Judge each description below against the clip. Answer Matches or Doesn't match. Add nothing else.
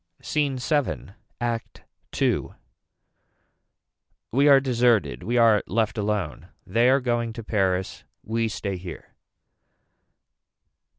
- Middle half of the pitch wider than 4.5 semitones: Doesn't match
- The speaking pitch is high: Doesn't match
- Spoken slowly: Matches